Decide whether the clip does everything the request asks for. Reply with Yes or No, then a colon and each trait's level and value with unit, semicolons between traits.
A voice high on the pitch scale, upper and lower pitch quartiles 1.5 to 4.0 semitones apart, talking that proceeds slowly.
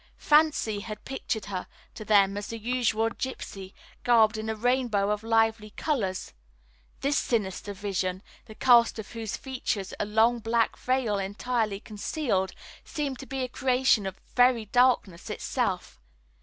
No: high, 225 Hz; average, 3.4 semitones; average, 150 wpm